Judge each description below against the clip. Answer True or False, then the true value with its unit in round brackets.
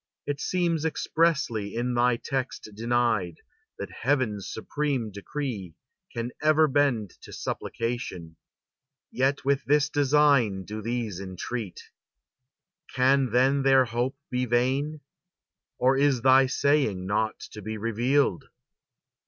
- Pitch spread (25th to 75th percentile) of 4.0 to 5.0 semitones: True (4.3 semitones)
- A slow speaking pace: True (115 wpm)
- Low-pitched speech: True (125 Hz)